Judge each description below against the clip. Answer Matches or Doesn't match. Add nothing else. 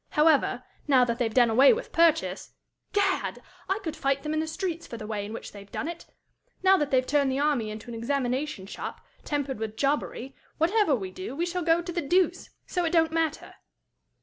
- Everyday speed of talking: Doesn't match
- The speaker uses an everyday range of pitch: Doesn't match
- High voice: Matches